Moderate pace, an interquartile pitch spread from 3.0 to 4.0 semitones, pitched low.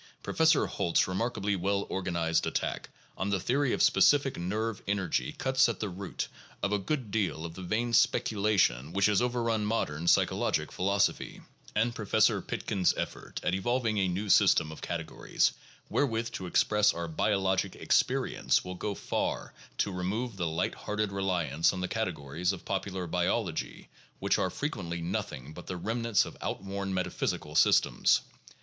Yes: average, 155 wpm; average, 3.5 semitones; low, 100 Hz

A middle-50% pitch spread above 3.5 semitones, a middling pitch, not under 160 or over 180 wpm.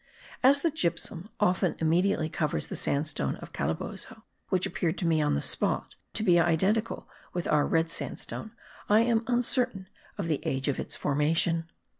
Yes: average, 5.3 semitones; medium, 170 Hz; average, 165 wpm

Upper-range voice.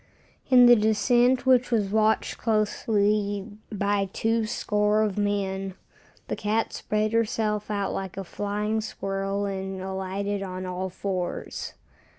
Yes: high, 205 Hz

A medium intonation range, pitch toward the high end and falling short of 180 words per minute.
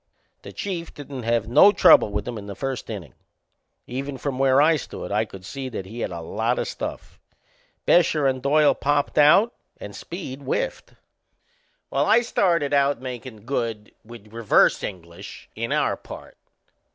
No: average, 4.6 semitones; low, 130 Hz; average, 165 wpm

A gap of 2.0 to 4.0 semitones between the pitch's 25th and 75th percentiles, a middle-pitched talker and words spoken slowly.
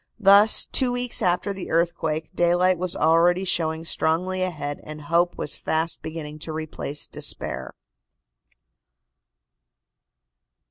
Yes: narrow, 2.6 semitones; medium, 170 Hz; slow, 110 wpm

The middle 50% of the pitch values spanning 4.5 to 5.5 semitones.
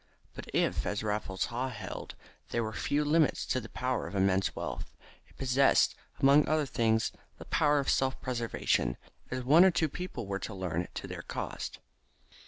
Yes: average, 5.2 semitones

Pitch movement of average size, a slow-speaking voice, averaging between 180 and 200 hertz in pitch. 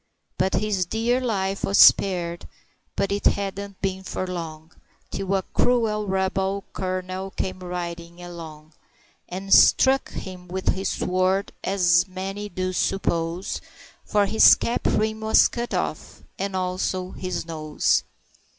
No: narrow, 1.8 semitones; slow, 130 wpm; high, 190 Hz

